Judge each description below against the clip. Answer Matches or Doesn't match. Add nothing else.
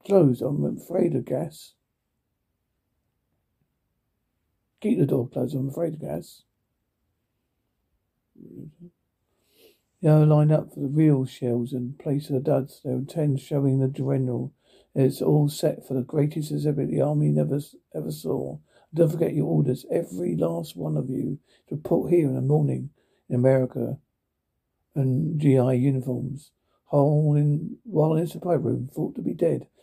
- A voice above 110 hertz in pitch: Matches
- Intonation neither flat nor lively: Matches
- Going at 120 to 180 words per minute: Matches